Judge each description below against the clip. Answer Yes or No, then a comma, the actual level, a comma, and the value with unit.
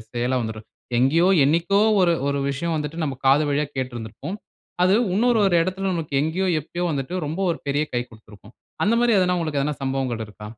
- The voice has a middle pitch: Yes, medium, 150 Hz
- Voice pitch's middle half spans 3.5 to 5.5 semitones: Yes, average, 5.2 semitones